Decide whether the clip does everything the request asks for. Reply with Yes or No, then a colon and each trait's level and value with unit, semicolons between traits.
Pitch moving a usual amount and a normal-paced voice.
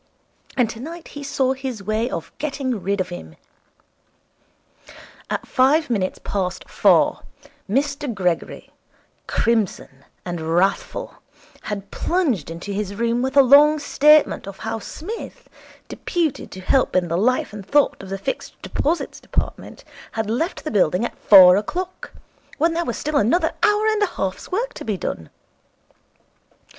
No: wide, 7.3 semitones; average, 150 wpm